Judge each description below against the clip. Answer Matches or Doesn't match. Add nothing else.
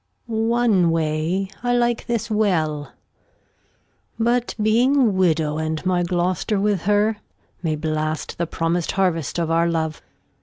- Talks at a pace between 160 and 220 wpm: Doesn't match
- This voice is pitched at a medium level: Matches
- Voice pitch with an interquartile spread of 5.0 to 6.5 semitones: Matches